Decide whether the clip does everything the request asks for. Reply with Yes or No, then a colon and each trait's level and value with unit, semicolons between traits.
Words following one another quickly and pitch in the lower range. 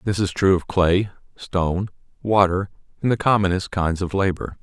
No: average, 170 wpm; very low, 95 Hz